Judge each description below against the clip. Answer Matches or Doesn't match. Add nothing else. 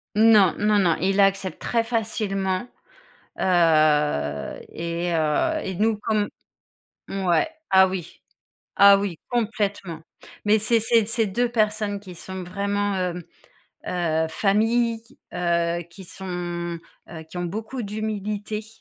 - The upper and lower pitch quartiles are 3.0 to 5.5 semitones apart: Matches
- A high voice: Matches